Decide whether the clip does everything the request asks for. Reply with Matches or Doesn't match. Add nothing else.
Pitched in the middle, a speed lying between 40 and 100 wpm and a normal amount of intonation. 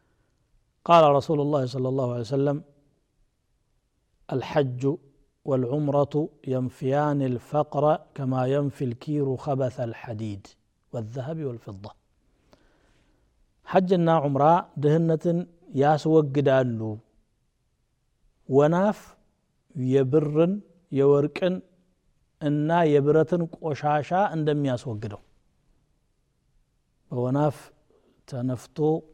Matches